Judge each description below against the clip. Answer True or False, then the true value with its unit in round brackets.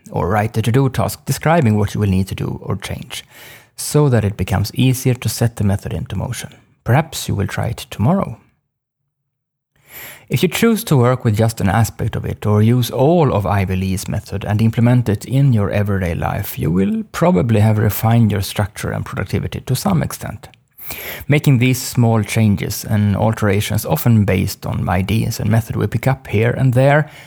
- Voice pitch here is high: False (115 Hz)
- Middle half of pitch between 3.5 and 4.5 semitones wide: True (4.1 semitones)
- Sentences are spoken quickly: False (190 wpm)